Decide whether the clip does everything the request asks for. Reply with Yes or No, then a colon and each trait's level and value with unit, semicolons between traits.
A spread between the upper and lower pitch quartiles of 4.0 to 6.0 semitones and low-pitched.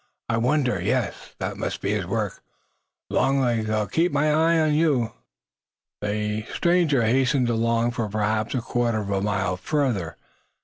Yes: average, 4.7 semitones; low, 115 Hz